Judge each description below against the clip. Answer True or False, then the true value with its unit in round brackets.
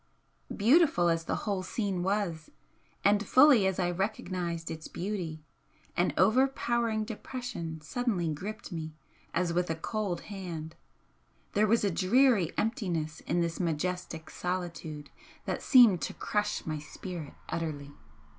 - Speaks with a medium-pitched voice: True (180 Hz)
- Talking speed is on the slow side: True (130 wpm)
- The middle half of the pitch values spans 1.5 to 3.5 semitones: False (4.4 semitones)